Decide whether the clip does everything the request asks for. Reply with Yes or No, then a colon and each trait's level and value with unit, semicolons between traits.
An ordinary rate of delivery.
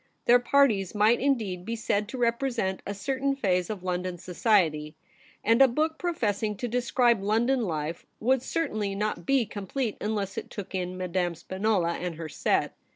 Yes: average, 165 wpm